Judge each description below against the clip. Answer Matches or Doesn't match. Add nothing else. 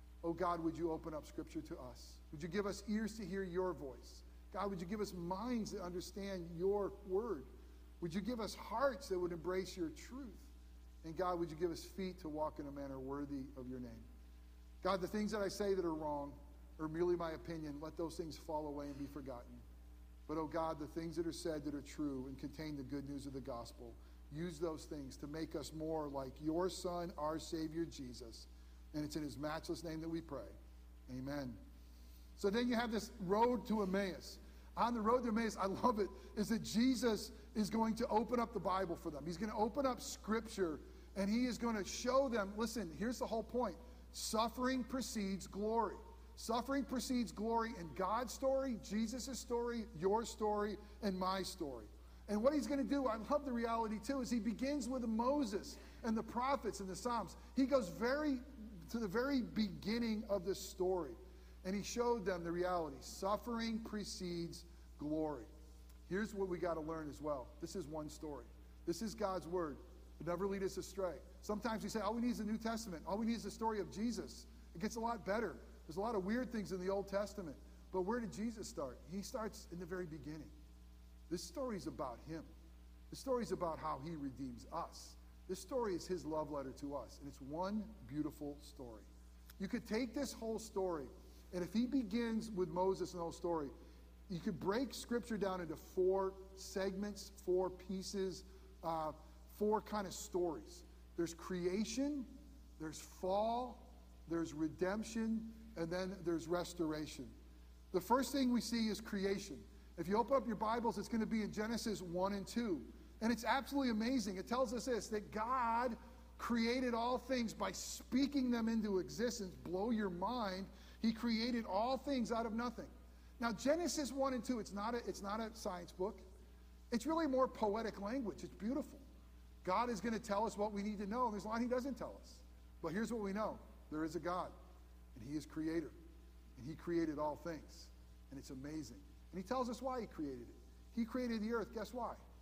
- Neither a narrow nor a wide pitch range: Doesn't match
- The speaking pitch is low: Doesn't match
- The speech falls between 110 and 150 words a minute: Doesn't match